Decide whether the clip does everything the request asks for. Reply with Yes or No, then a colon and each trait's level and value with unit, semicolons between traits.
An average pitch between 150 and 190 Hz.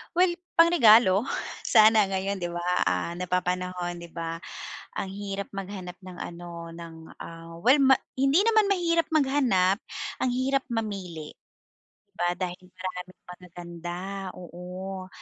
Yes: medium, 185 Hz